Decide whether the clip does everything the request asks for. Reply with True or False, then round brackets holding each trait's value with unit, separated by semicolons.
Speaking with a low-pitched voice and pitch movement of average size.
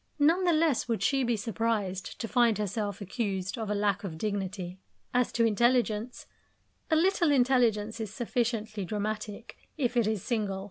False (220 Hz; 3.2 semitones)